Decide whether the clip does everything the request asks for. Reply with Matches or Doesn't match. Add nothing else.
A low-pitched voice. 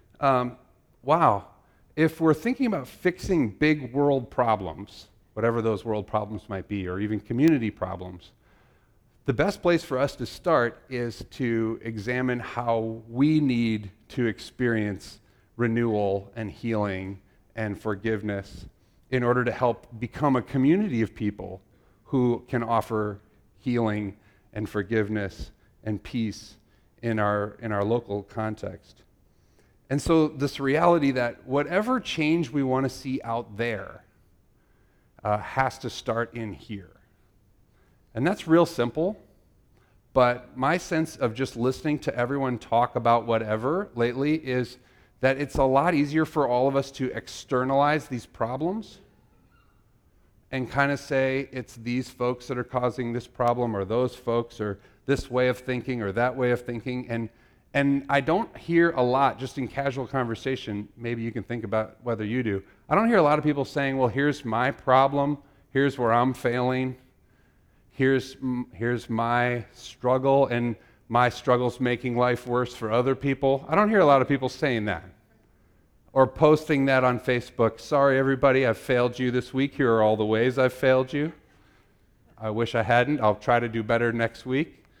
Matches